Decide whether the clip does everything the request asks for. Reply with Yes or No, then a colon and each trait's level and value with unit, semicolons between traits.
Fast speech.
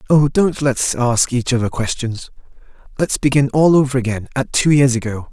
No: average, 170 wpm